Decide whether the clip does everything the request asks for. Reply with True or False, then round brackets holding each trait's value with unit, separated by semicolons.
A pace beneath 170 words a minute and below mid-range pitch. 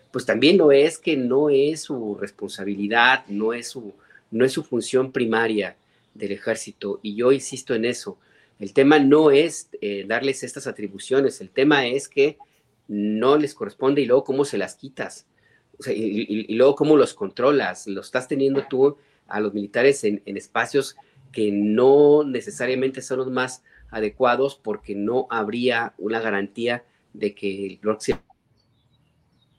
True (160 wpm; 120 Hz)